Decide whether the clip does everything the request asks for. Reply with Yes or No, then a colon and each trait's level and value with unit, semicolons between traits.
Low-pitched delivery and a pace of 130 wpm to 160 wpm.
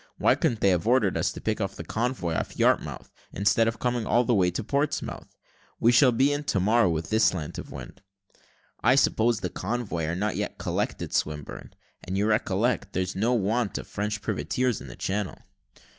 No: low, 105 Hz; average, 195 wpm